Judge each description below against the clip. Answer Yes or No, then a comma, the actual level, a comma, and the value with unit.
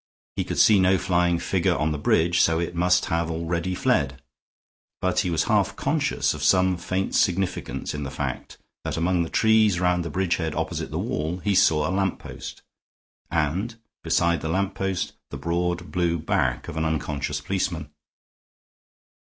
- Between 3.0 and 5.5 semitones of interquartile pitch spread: No, narrow, 2.4 semitones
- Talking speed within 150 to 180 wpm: Yes, average, 170 wpm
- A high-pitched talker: No, very low, 85 Hz